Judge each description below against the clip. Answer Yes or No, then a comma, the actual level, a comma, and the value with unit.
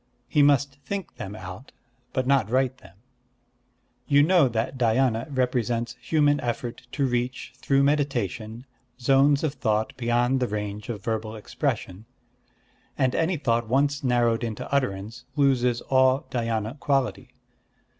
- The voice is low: Yes, low, 125 Hz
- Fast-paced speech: No, slow, 135 wpm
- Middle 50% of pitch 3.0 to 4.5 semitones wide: Yes, average, 3.3 semitones